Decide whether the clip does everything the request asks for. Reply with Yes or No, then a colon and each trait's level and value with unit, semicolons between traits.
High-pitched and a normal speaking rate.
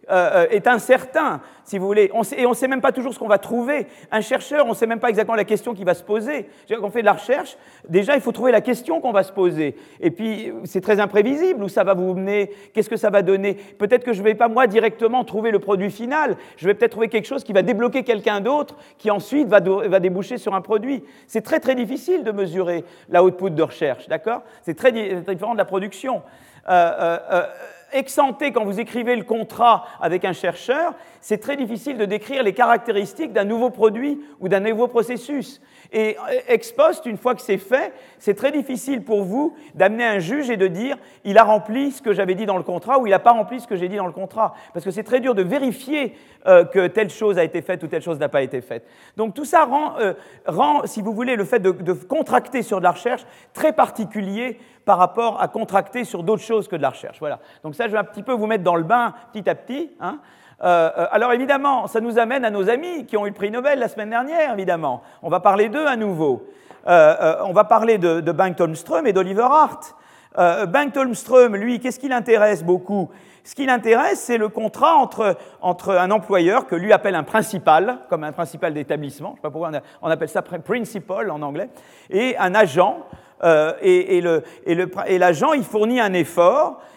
No: high, 220 Hz; fast, 235 wpm